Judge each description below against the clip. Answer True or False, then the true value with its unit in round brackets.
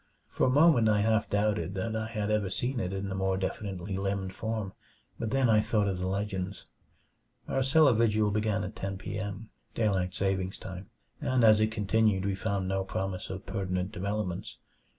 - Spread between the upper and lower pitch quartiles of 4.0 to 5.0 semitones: False (2.4 semitones)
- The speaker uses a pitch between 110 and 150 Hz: False (100 Hz)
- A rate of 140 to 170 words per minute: False (190 wpm)